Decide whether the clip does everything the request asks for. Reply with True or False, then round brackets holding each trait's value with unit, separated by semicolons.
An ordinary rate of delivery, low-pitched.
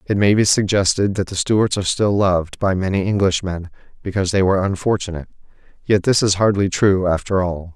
True (185 wpm; 95 Hz)